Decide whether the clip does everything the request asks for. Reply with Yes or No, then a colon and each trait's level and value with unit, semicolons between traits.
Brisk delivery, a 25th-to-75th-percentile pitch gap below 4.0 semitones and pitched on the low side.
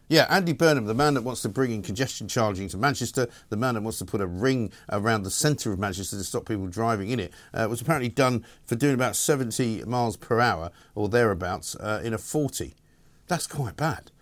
Yes: fast, 225 wpm; average, 3.5 semitones; low, 115 Hz